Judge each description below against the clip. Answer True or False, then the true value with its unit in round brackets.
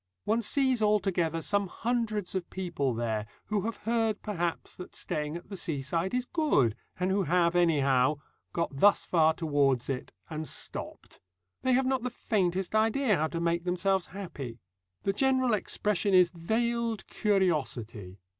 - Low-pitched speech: False (185 Hz)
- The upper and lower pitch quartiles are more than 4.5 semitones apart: True (5.5 semitones)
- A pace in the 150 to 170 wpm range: True (155 wpm)